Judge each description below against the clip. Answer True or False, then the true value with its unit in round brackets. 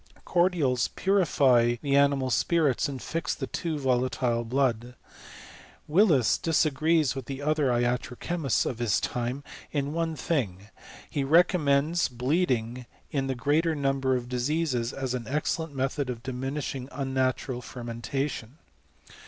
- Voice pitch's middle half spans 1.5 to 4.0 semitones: True (3.5 semitones)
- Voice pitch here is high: False (135 Hz)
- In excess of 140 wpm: False (135 wpm)